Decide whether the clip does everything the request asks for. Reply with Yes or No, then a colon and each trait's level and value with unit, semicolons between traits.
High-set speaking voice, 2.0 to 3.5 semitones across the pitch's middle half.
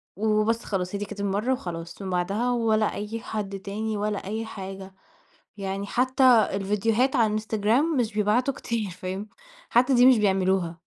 Yes: high, 210 Hz; average, 2.8 semitones